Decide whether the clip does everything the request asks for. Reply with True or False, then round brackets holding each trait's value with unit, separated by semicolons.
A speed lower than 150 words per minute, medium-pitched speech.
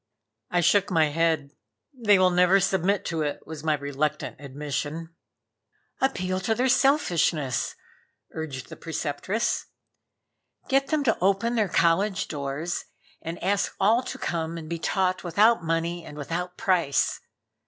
True (140 wpm; 175 Hz)